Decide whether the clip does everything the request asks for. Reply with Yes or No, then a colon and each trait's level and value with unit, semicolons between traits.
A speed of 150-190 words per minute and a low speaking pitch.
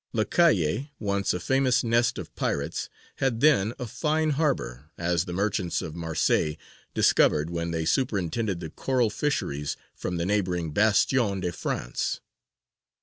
No: average, 140 wpm; low, 100 Hz